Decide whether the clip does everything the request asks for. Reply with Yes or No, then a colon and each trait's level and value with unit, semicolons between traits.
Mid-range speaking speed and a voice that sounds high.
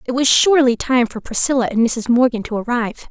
No: fast, 210 wpm; high, 245 Hz